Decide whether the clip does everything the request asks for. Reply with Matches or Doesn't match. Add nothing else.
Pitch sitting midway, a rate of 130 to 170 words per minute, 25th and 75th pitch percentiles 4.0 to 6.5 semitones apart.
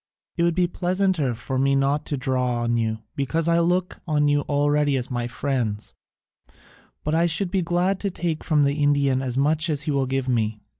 Doesn't match